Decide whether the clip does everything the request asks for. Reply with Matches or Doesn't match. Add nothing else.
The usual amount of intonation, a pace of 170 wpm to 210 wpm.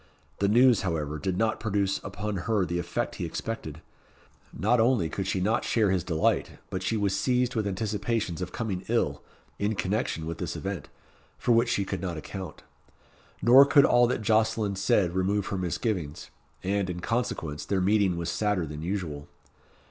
Matches